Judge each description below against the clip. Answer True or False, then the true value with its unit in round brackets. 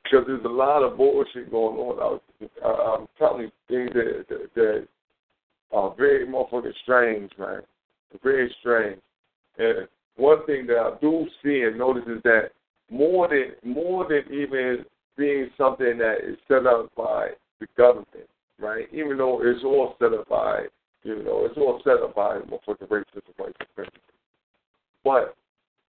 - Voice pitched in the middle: True (155 Hz)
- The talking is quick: False (160 wpm)